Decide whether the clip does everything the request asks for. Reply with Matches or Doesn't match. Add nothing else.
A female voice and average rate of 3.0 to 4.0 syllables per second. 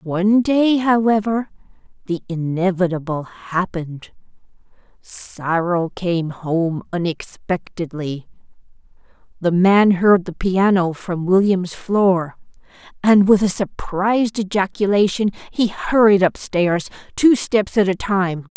Matches